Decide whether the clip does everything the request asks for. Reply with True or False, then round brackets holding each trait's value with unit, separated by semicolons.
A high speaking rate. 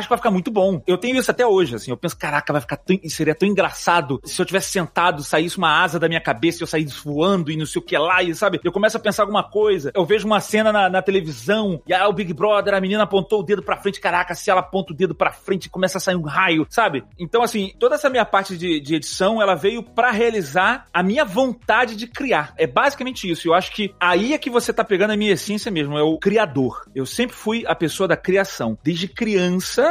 True (255 wpm)